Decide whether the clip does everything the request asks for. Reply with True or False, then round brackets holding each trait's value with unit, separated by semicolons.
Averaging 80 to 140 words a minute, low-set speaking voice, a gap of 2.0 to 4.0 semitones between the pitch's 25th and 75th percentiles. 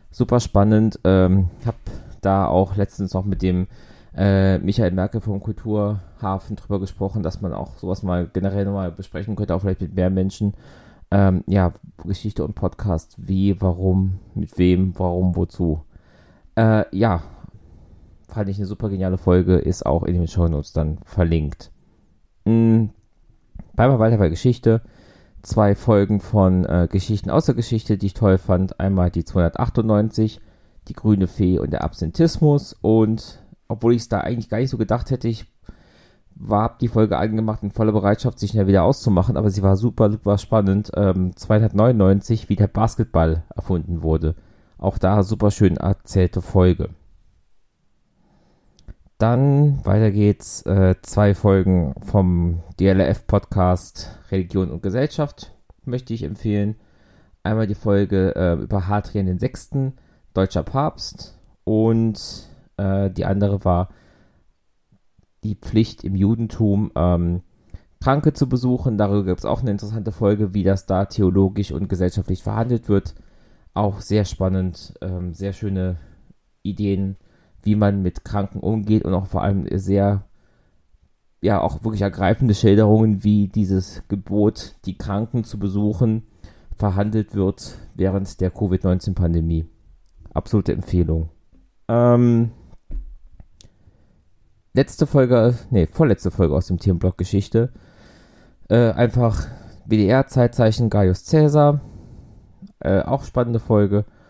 True (135 wpm; 100 Hz; 3.0 semitones)